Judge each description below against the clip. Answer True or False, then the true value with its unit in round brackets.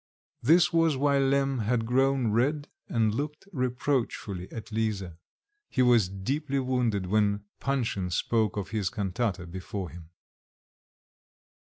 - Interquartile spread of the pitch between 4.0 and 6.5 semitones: True (5.1 semitones)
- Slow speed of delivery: True (125 wpm)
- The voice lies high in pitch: False (115 Hz)